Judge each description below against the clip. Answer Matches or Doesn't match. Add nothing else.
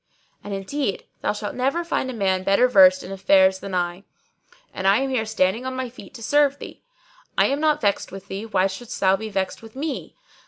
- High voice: Matches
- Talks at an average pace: Doesn't match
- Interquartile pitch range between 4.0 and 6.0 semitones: Matches